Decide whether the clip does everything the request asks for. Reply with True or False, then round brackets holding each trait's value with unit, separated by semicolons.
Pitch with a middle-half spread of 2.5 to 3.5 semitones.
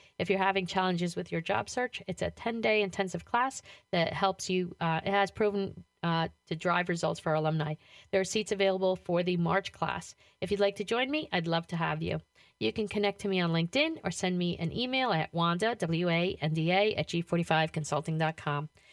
True (3.2 semitones)